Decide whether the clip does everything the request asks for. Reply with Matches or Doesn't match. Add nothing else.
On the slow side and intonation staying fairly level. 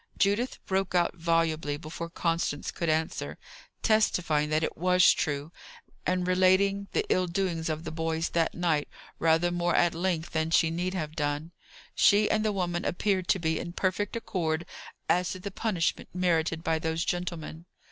Doesn't match